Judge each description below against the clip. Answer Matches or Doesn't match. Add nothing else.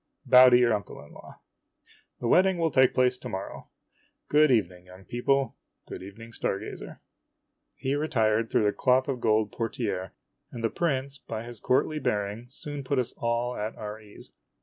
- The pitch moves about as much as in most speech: Matches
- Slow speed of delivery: Doesn't match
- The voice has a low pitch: Matches